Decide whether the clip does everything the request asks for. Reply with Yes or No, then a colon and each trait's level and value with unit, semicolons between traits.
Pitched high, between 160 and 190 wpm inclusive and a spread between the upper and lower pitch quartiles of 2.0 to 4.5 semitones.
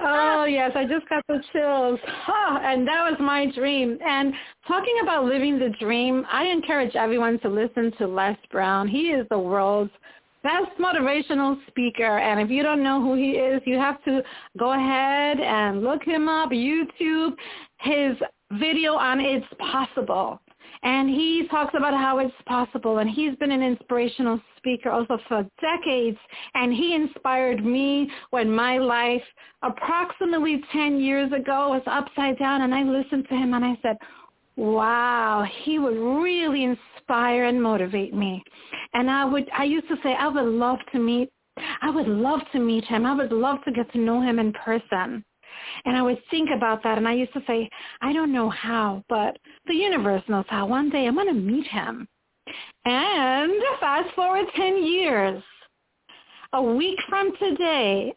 Yes: very high, 265 Hz; average, 170 wpm; average, 3.7 semitones